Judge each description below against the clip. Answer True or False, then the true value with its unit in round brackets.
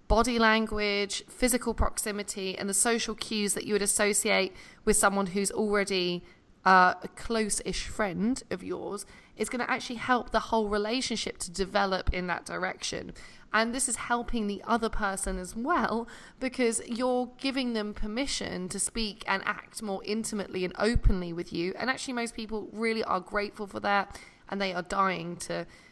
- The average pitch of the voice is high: True (210 Hz)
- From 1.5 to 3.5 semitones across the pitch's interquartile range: True (2.8 semitones)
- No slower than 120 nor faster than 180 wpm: True (170 wpm)